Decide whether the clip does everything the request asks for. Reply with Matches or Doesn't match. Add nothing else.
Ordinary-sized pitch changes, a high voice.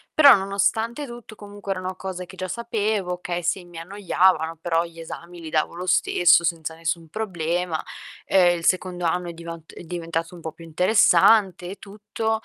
Doesn't match